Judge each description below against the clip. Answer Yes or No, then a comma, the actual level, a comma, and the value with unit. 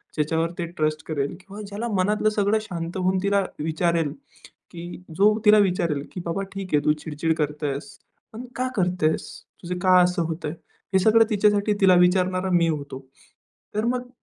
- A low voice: No, medium, 180 Hz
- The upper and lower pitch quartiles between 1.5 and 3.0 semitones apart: No, average, 3.9 semitones